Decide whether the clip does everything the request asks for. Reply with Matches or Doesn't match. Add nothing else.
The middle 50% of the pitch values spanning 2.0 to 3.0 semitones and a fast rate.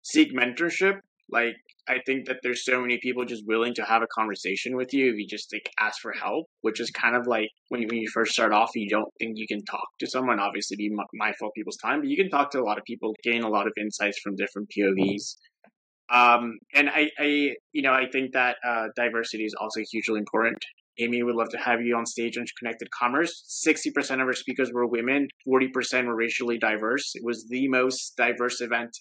Matches